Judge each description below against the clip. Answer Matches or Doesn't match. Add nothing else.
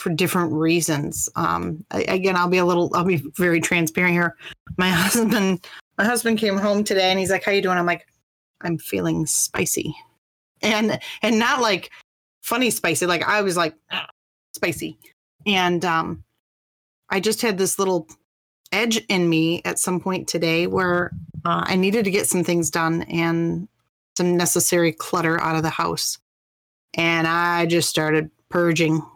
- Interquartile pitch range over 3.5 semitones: Doesn't match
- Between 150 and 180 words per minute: Matches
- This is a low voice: Doesn't match